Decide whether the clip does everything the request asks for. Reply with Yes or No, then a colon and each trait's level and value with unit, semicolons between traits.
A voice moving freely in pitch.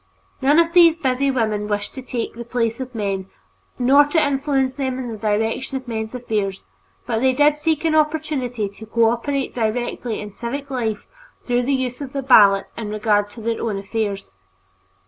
No: average, 3.9 semitones